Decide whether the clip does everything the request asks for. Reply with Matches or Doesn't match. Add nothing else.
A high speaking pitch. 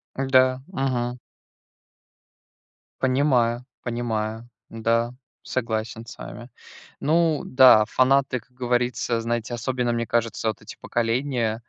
Doesn't match